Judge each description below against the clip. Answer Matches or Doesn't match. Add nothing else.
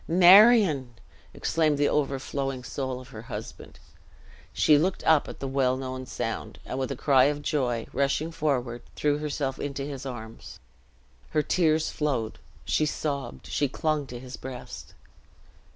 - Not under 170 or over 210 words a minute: Doesn't match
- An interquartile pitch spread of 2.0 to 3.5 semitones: Matches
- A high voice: Doesn't match